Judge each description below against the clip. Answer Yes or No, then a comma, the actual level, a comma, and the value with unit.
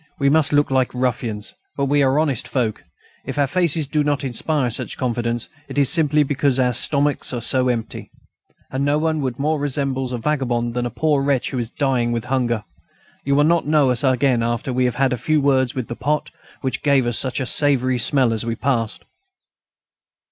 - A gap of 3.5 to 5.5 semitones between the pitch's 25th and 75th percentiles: No, average, 2.9 semitones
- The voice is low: Yes, low, 130 Hz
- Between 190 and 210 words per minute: Yes, fast, 205 wpm